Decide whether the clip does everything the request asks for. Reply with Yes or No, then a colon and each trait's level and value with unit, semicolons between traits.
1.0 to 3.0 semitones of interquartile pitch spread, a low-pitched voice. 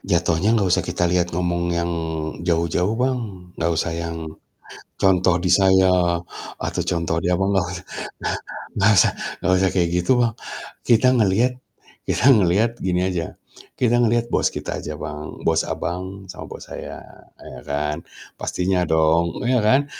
No: average, 3.7 semitones; very low, 90 Hz